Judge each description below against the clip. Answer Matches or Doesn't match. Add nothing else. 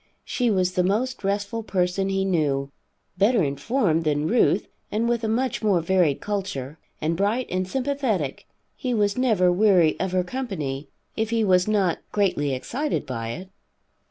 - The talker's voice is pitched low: Doesn't match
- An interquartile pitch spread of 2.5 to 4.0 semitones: Doesn't match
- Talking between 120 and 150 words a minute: Doesn't match